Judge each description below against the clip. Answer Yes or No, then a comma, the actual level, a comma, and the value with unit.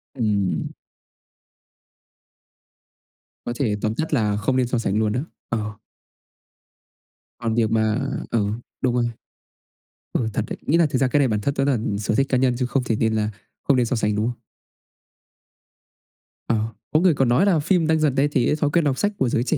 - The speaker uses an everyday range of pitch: Yes, average, 4.3 semitones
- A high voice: No, low, 125 Hz